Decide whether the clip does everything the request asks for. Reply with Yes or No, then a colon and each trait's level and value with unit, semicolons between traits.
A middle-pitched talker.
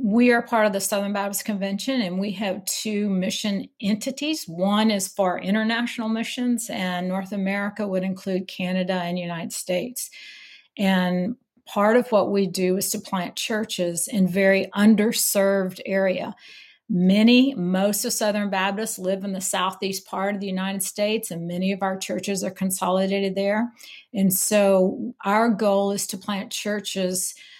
No: high, 200 Hz